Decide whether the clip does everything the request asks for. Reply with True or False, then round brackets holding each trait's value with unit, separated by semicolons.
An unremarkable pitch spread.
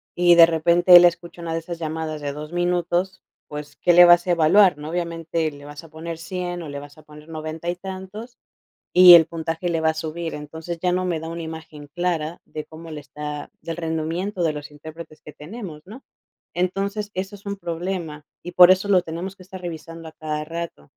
False (2.1 semitones)